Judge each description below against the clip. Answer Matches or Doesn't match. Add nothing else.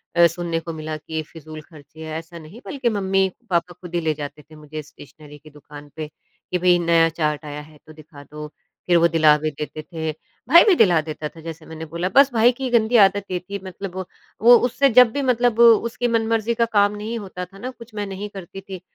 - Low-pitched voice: Doesn't match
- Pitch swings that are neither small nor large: Doesn't match